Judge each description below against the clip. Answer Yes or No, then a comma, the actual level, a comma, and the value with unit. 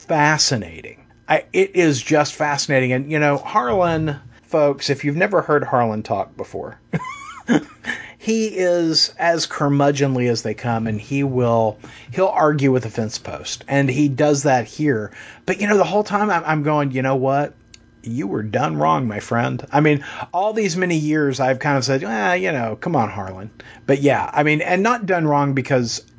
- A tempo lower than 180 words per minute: No, average, 190 wpm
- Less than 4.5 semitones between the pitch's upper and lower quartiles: Yes, average, 3.6 semitones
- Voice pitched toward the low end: No, medium, 145 Hz